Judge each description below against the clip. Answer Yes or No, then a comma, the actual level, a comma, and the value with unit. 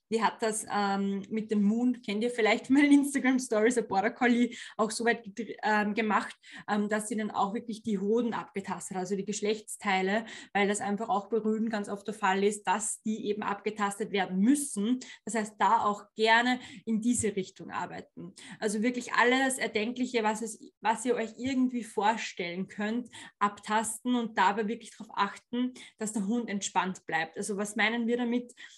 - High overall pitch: Yes, high, 220 Hz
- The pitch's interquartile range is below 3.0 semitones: Yes, narrow, 2.4 semitones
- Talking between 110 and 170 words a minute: No, average, 180 wpm